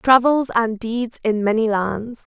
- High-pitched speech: Yes, high, 230 Hz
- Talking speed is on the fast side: No, average, 155 wpm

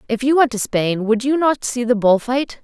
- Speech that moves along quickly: Yes, fast, 275 wpm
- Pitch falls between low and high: No, high, 245 Hz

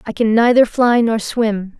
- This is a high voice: Yes, high, 225 Hz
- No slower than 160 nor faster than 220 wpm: Yes, average, 200 wpm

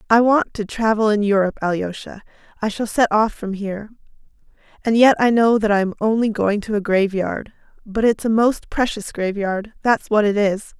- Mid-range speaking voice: No, high, 210 Hz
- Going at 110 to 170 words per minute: No, average, 195 wpm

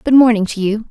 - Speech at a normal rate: No, fast, 265 wpm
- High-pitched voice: Yes, high, 220 Hz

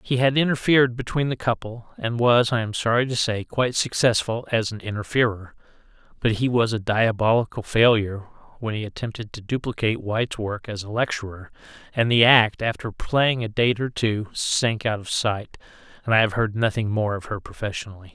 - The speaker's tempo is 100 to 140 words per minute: No, average, 180 wpm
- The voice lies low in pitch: Yes, low, 115 Hz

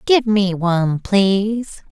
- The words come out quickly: No, slow, 125 wpm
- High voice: Yes, high, 200 Hz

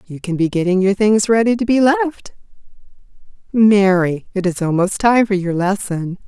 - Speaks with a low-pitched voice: No, high, 200 Hz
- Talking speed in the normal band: Yes, average, 170 wpm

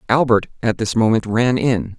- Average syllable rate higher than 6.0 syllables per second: No, 4.7 syllables/s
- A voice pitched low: Yes, low, 115 Hz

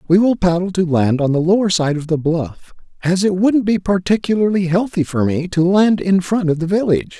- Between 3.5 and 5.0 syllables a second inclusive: No, 5.4 syllables/s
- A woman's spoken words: No, male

